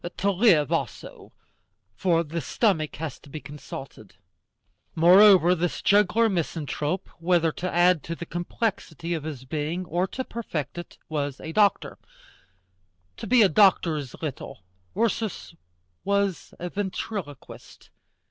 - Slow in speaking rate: Yes, slow, 130 wpm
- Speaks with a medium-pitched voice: Yes, medium, 175 Hz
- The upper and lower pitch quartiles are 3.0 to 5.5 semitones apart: Yes, average, 4.3 semitones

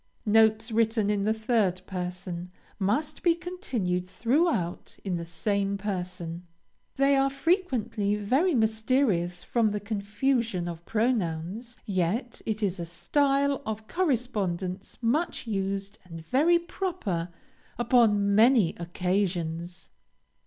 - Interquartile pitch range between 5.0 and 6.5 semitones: Yes, wide, 5.5 semitones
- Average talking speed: No, slow, 115 wpm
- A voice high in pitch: Yes, high, 210 Hz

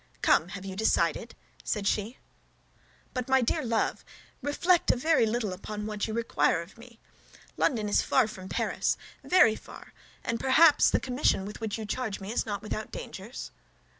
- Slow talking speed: No, average, 165 wpm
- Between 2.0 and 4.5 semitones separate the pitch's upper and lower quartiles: Yes, average, 3.4 semitones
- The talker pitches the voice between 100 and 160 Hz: No, high, 220 Hz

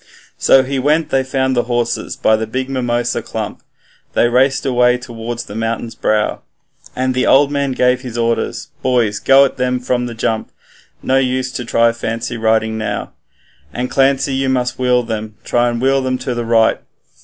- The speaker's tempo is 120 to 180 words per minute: No, average, 190 wpm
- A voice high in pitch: No, low, 125 Hz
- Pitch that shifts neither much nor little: No, narrow, 2.2 semitones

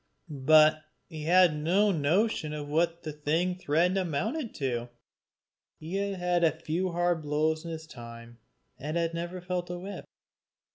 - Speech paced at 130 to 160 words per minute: Yes, average, 150 wpm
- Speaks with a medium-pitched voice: Yes, medium, 165 Hz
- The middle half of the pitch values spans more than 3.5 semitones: No, average, 2.9 semitones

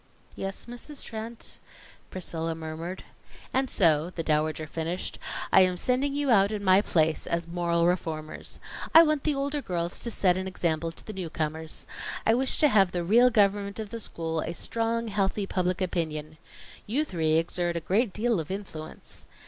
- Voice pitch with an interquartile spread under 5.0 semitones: No, average, 5.3 semitones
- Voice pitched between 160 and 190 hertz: Yes, medium, 185 Hz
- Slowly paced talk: No, average, 175 wpm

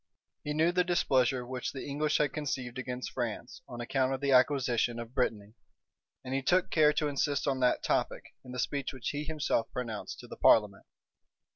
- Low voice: Yes, low, 130 Hz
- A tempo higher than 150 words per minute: Yes, average, 190 wpm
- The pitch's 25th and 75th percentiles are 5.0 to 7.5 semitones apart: No, average, 3.1 semitones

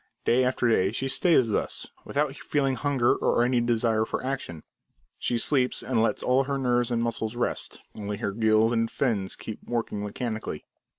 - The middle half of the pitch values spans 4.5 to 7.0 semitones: No, average, 2.8 semitones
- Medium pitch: No, low, 120 Hz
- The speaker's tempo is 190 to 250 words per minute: No, average, 175 wpm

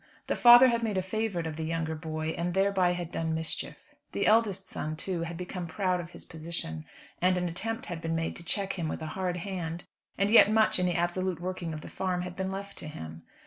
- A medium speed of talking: No, fast, 235 wpm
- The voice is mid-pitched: Yes, medium, 180 Hz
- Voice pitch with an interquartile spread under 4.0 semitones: Yes, average, 2.9 semitones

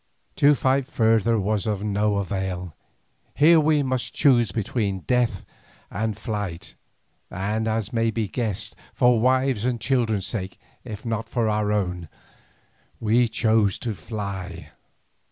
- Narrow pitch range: No, average, 3.2 semitones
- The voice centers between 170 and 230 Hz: No, low, 110 Hz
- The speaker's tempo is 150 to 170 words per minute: No, slow, 135 wpm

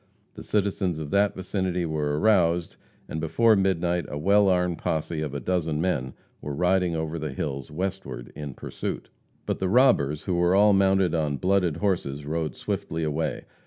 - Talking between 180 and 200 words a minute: No, average, 170 wpm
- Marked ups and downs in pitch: No, average, 3.9 semitones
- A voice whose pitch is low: Yes, very low, 85 Hz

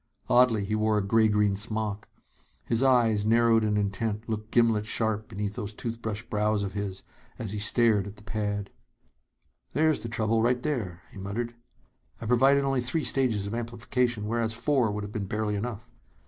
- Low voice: Yes, low, 110 Hz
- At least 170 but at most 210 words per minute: Yes, average, 175 wpm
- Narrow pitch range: Yes, narrow, 2.2 semitones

